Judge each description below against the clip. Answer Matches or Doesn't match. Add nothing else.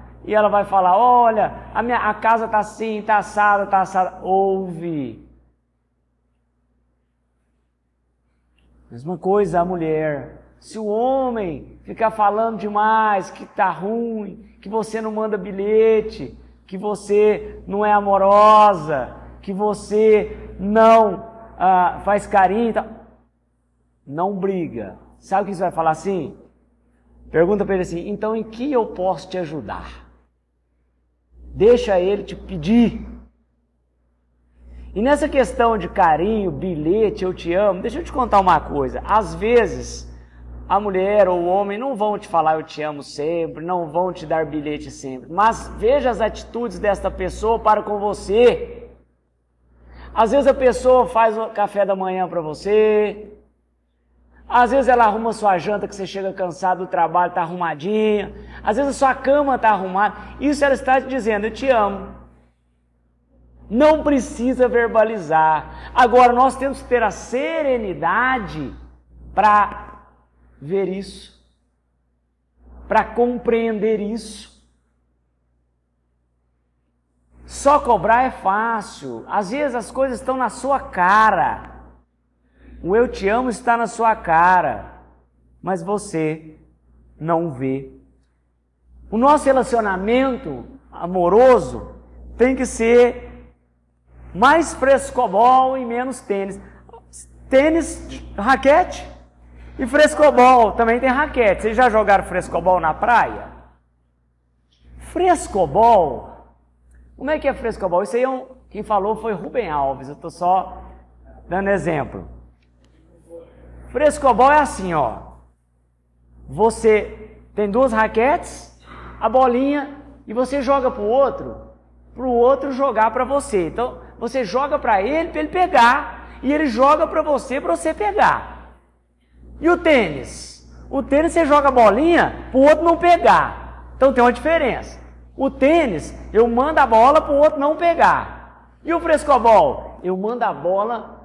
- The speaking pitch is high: Matches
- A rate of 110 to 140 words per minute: Matches